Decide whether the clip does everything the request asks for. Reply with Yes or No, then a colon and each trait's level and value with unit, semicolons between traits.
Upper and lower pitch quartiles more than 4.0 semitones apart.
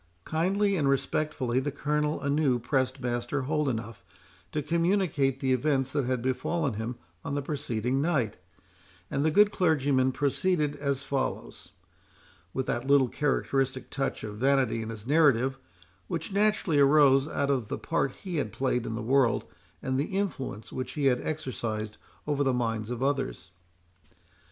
No: average, 3.3 semitones